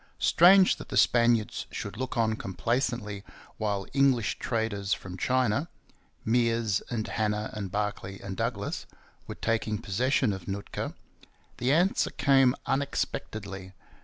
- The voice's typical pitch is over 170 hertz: No, low, 110 Hz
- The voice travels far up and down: No, average, 3.9 semitones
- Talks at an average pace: No, slow, 125 wpm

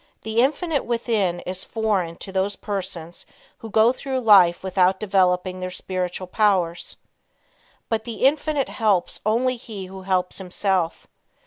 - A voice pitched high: Yes, high, 195 Hz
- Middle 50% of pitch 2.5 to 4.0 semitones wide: Yes, average, 3.6 semitones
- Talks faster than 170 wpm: No, slow, 135 wpm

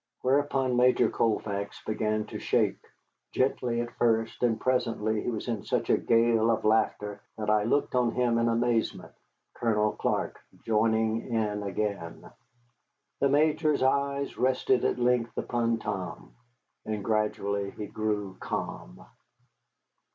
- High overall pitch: No, low, 115 Hz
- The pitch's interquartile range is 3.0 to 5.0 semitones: No, narrow, 2.6 semitones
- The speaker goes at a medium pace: No, slow, 130 wpm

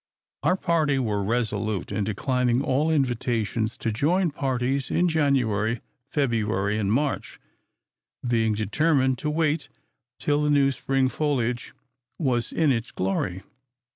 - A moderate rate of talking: No, slow, 125 wpm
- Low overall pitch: Yes, low, 125 Hz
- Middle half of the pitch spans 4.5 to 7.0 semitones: Yes, average, 4.9 semitones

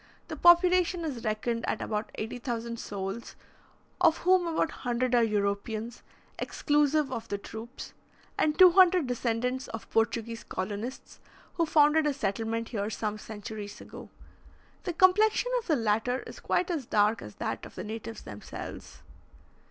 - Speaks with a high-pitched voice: Yes, high, 235 Hz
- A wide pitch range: Yes, wide, 6.2 semitones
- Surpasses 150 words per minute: No, average, 145 wpm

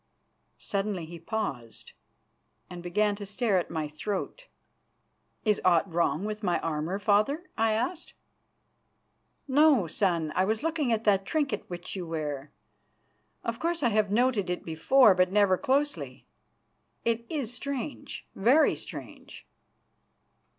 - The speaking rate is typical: No, slow, 130 wpm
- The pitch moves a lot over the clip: Yes, wide, 5.7 semitones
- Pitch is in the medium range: No, high, 205 Hz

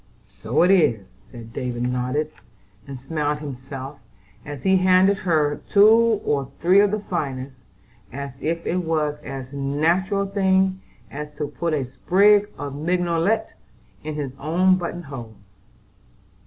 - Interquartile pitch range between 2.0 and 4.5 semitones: No, wide, 5.4 semitones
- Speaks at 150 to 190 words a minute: No, average, 140 wpm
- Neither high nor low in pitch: Yes, medium, 150 Hz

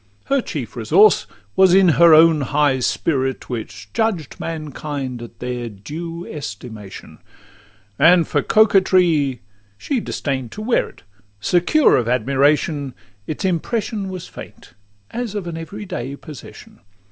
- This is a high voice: No, medium, 155 Hz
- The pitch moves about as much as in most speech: No, wide, 6.2 semitones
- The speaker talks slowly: Yes, slow, 130 wpm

